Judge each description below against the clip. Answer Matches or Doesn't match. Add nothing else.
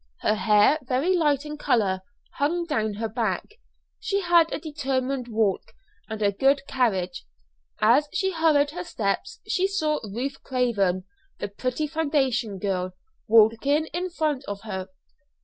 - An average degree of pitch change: Doesn't match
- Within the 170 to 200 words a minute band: Doesn't match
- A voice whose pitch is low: Doesn't match